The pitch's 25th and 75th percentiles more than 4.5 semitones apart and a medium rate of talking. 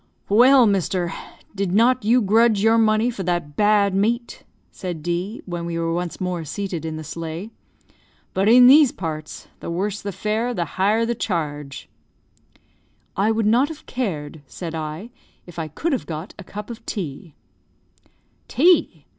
Yes: average, 5.2 semitones; average, 165 wpm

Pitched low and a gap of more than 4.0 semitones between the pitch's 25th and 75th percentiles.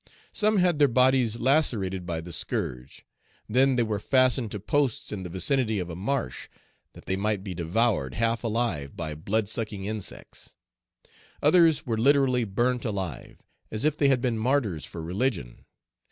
Yes: low, 110 Hz; wide, 5.6 semitones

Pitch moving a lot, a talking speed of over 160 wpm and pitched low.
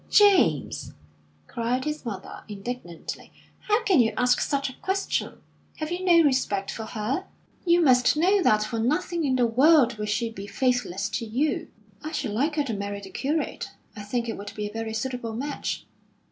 No: wide, 6.0 semitones; average, 185 wpm; very high, 250 Hz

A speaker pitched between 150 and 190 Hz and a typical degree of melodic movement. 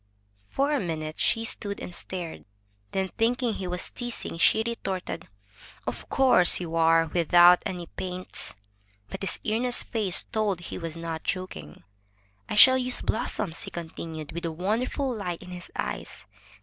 Yes: medium, 185 Hz; average, 5.0 semitones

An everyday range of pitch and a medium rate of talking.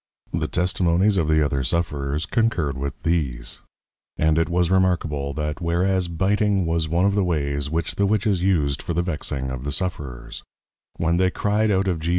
Yes: average, 4.3 semitones; average, 180 wpm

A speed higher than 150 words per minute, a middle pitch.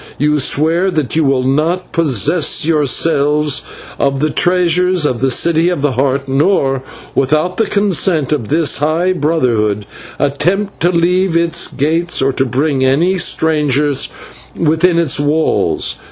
No: average, 140 wpm; medium, 155 Hz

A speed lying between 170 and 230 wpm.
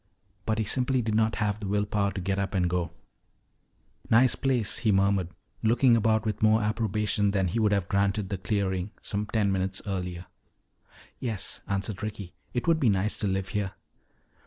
Yes: average, 185 wpm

